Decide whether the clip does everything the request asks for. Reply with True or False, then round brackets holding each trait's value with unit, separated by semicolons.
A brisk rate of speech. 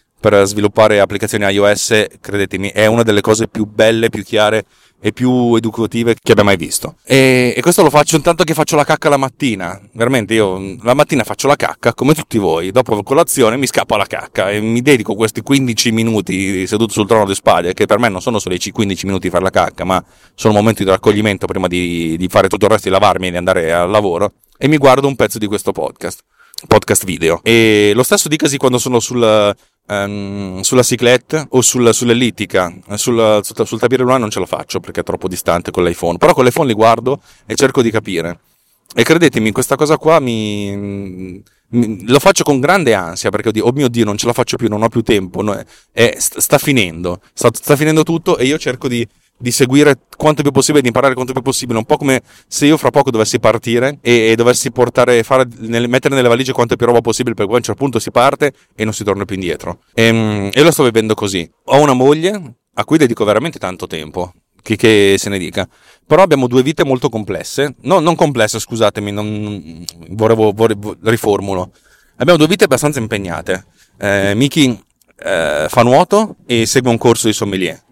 True (210 wpm)